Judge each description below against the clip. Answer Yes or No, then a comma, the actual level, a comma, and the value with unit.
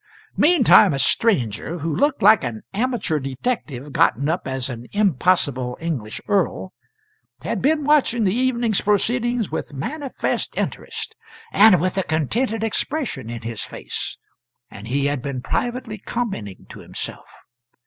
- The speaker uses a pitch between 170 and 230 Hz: Yes, medium, 185 Hz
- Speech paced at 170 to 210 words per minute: No, average, 140 wpm